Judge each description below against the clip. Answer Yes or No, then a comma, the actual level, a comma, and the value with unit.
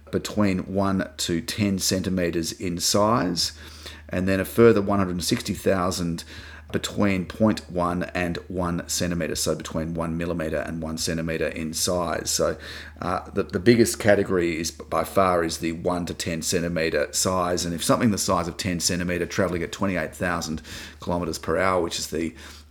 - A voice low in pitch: Yes, very low, 90 Hz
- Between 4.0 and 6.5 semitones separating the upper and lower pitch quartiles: No, average, 2.7 semitones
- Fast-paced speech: No, average, 155 wpm